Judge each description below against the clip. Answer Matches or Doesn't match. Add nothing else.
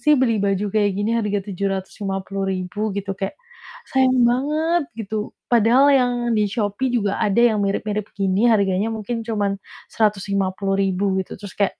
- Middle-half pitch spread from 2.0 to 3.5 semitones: Matches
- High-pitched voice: Matches